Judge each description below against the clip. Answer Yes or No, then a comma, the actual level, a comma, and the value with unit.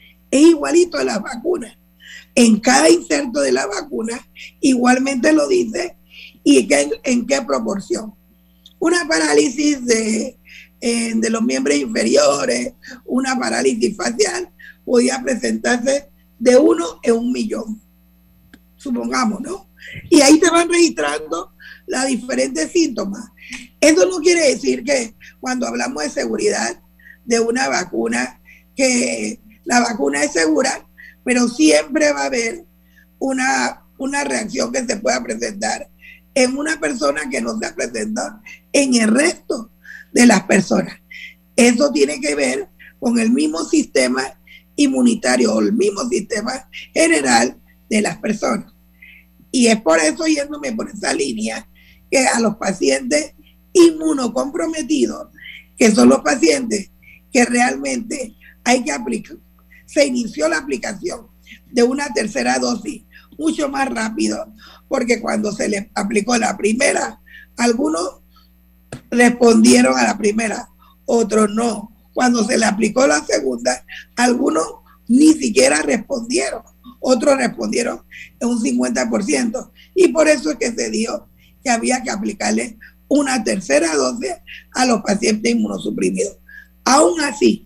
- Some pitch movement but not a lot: No, wide, 6.8 semitones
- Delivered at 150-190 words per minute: No, average, 130 wpm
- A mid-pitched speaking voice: No, high, 240 Hz